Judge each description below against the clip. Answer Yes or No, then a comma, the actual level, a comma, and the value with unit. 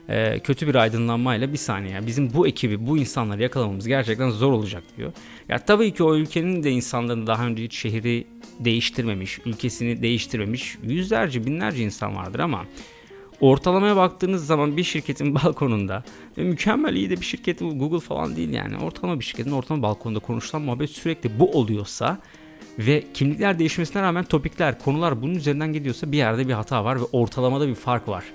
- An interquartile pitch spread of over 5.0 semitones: Yes, wide, 5.4 semitones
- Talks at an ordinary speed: No, fast, 165 wpm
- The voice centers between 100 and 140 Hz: Yes, low, 135 Hz